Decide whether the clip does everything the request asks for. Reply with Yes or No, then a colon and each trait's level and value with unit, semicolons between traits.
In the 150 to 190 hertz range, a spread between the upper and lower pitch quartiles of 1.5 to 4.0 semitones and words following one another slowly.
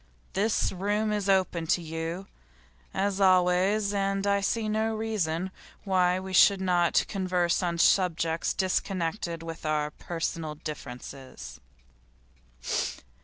Yes: medium, 185 Hz; average, 3.1 semitones; slow, 115 wpm